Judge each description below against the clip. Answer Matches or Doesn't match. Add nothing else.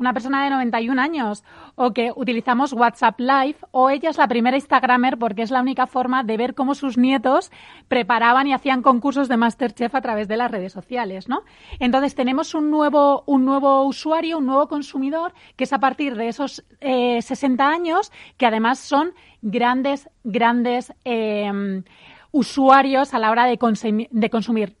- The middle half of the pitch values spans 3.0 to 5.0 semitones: Doesn't match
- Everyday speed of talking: Matches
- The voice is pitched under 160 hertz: Doesn't match